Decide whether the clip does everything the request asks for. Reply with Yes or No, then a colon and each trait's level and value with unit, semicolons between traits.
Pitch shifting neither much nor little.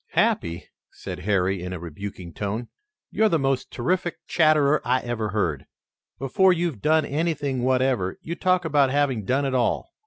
No: wide, 7.0 semitones